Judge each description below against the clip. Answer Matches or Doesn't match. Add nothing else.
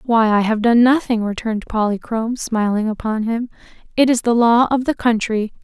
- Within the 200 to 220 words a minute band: Doesn't match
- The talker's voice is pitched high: Matches